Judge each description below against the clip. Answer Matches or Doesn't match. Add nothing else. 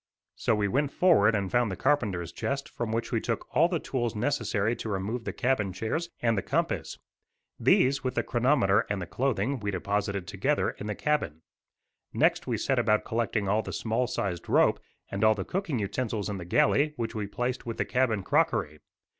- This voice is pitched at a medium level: Doesn't match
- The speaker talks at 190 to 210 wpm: Matches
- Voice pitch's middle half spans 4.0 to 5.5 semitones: Matches